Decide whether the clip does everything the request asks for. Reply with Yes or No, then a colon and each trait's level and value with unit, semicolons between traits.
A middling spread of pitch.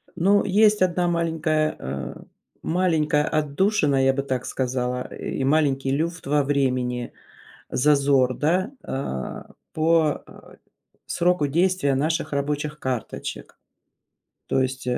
Yes: average, 3.9 semitones